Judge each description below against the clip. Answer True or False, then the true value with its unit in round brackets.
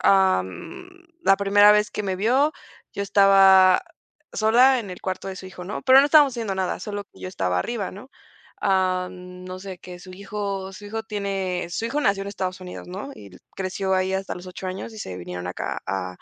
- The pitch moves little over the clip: True (2.3 semitones)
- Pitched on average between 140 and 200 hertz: True (190 Hz)